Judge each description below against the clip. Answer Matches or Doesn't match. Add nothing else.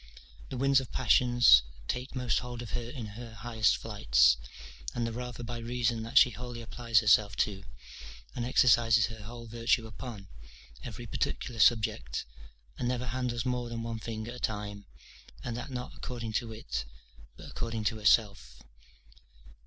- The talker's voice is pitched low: Matches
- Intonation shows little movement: Matches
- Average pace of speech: Matches